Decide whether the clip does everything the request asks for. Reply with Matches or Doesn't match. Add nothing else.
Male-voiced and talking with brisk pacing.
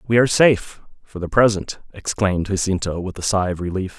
Doesn't match